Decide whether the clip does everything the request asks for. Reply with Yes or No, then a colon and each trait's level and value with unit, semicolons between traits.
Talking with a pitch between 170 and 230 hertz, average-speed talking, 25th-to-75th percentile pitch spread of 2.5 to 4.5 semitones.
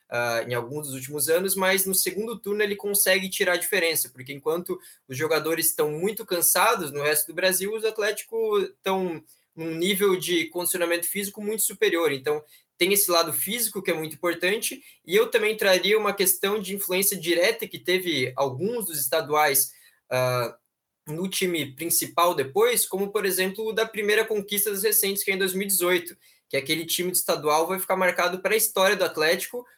Yes: medium, 185 Hz; average, 175 wpm; average, 4.0 semitones